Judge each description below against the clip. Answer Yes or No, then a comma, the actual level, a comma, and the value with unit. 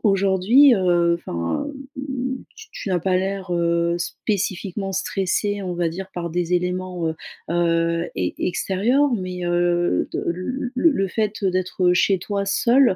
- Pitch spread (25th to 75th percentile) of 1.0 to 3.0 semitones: Yes, average, 2.7 semitones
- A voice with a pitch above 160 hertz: Yes, medium, 185 Hz